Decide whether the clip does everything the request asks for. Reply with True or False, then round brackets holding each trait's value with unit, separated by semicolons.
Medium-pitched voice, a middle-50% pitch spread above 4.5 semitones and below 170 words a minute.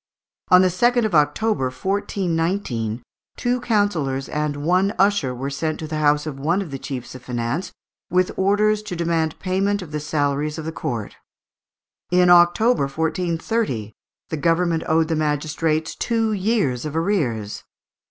True (160 Hz; 5.0 semitones; 150 wpm)